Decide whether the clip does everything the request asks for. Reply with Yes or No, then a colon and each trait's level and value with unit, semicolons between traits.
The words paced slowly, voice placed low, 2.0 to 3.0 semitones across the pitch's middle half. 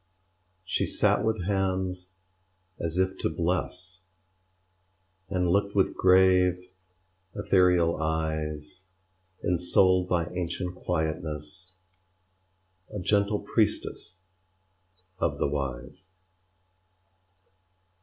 Yes: slow, 80 wpm; very low, 90 Hz; average, 2.7 semitones